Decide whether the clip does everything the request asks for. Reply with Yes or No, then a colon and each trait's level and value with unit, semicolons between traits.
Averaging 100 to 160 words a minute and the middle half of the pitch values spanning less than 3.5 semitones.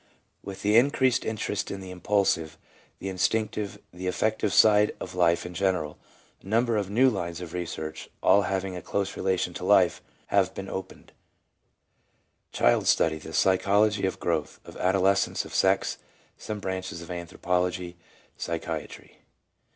Yes: average, 150 wpm; narrow, 2.6 semitones